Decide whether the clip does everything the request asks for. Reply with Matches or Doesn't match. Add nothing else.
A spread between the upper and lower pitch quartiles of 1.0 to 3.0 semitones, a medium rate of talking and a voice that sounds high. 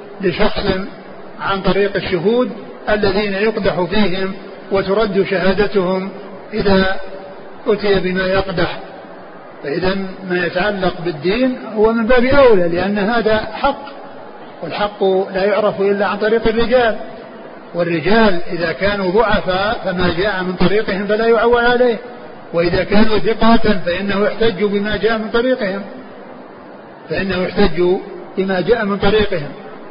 Matches